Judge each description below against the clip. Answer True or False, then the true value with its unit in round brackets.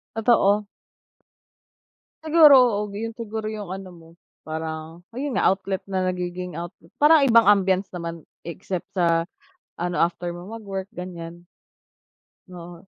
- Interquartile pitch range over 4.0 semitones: False (3.7 semitones)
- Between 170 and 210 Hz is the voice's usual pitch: True (185 Hz)